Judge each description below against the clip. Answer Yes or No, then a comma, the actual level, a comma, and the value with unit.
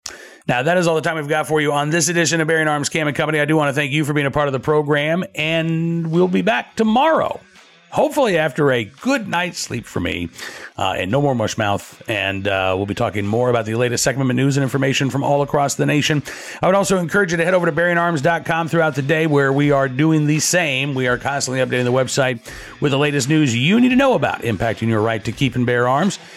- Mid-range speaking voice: Yes, medium, 150 Hz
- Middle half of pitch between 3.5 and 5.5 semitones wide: Yes, average, 4.3 semitones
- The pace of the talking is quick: Yes, fast, 255 wpm